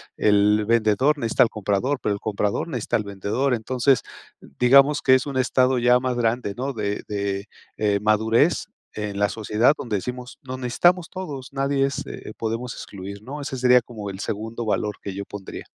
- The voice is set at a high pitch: No, low, 115 Hz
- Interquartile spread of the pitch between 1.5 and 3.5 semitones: No, average, 3.9 semitones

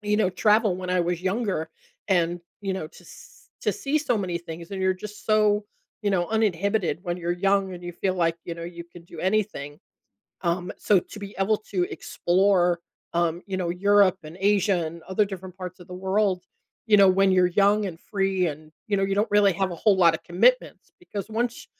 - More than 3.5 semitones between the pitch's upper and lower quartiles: No, average, 2.7 semitones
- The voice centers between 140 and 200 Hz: Yes, high, 190 Hz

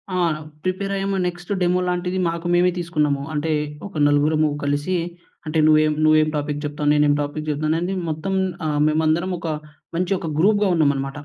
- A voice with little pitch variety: No, average, 3.1 semitones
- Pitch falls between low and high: Yes, medium, 155 Hz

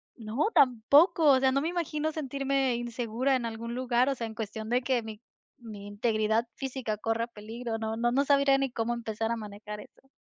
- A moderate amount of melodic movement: Yes, average, 3.4 semitones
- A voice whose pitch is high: Yes, high, 240 Hz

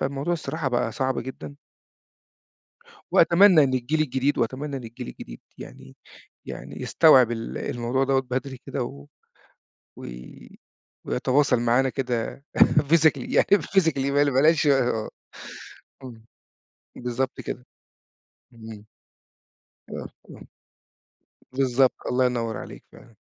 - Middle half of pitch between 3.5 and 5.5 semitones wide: No, average, 2.8 semitones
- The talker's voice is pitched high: No, low, 130 Hz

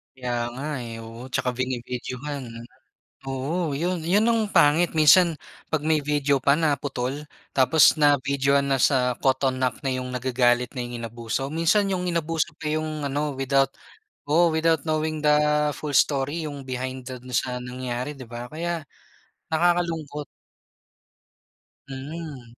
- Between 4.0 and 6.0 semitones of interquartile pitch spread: No, average, 3.5 semitones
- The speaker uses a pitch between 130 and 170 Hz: Yes, medium, 140 Hz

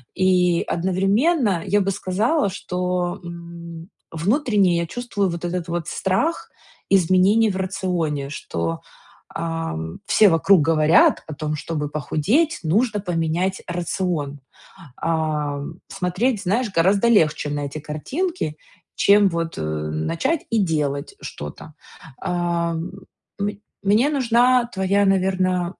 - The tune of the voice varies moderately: Yes, average, 3.7 semitones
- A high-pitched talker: No, medium, 180 Hz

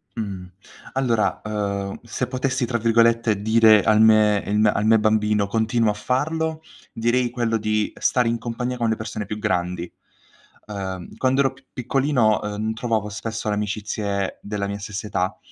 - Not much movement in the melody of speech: Yes, narrow, 2.3 semitones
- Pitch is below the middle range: Yes, low, 110 Hz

